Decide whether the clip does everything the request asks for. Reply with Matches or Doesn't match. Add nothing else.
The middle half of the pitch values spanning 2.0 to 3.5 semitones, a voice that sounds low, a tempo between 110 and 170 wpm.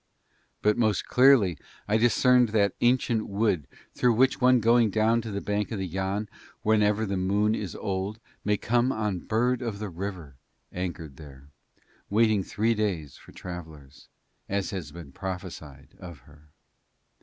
Doesn't match